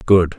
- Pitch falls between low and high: No, very low, 85 Hz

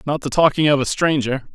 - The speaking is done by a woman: No, male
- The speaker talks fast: No, average, 195 wpm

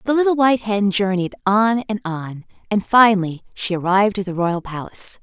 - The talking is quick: No, average, 185 wpm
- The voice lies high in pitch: Yes, high, 200 Hz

